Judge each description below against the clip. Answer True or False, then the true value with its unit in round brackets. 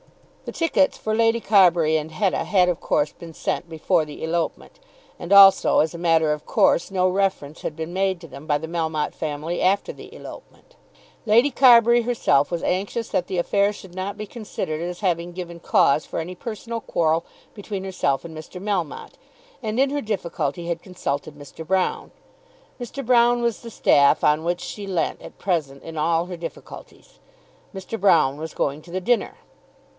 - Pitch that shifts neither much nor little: True (4.2 semitones)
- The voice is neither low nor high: True (175 Hz)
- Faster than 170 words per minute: True (180 wpm)